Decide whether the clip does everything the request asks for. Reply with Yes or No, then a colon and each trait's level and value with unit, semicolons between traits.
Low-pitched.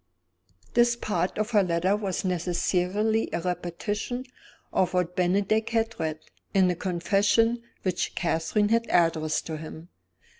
No: medium, 185 Hz